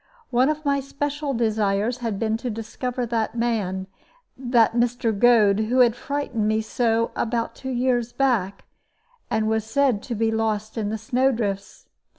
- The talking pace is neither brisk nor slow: Yes, average, 160 wpm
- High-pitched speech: Yes, high, 230 Hz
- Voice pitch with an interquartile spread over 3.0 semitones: No, narrow, 2.4 semitones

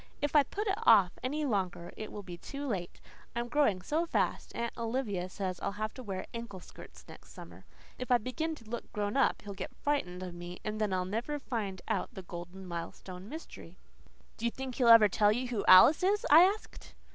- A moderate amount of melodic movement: No, wide, 6.1 semitones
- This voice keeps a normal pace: No, fast, 215 wpm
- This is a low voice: No, high, 215 Hz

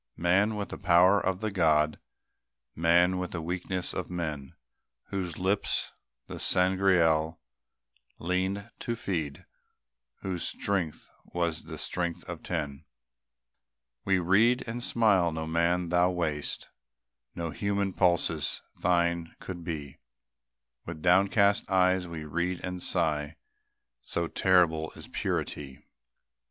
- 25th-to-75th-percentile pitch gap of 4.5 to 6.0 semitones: No, narrow, 2.5 semitones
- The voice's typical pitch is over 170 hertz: No, very low, 90 Hz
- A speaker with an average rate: No, slow, 120 wpm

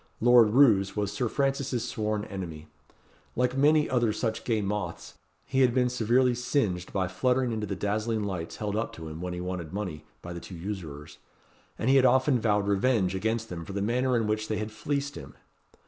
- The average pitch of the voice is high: No, low, 110 Hz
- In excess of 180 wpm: Yes, average, 200 wpm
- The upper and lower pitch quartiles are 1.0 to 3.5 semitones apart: No, average, 4.6 semitones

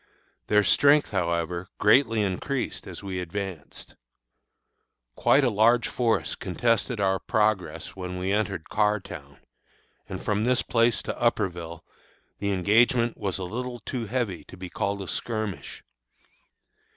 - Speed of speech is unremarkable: No, slow, 130 wpm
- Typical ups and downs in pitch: Yes, average, 4.0 semitones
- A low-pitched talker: Yes, low, 105 Hz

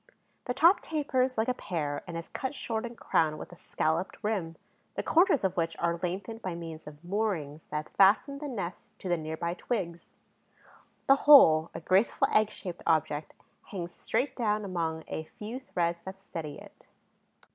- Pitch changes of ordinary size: No, wide, 5.7 semitones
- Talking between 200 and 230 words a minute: No, average, 180 wpm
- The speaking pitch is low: No, medium, 185 Hz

